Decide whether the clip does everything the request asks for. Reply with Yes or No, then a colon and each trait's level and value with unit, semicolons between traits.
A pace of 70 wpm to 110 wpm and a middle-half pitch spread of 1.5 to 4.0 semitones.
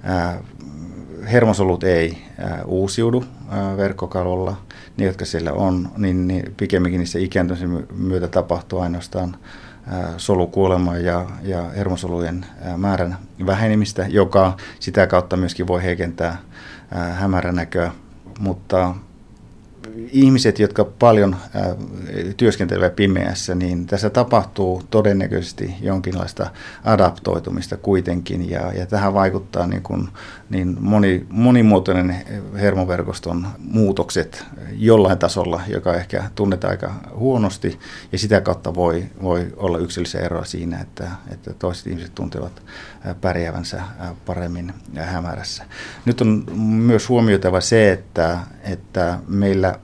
Yes: average, 105 wpm; narrow, 2.4 semitones